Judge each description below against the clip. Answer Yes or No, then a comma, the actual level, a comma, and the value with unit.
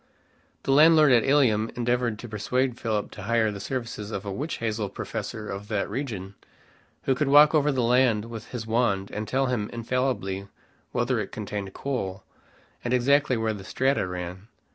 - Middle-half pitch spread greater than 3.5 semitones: Yes, average, 3.9 semitones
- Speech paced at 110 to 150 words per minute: No, average, 175 wpm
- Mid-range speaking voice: No, low, 115 Hz